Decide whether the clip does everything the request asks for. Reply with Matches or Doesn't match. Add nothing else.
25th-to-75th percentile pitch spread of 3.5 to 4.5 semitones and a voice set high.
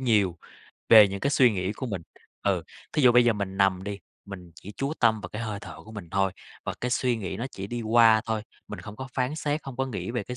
Doesn't match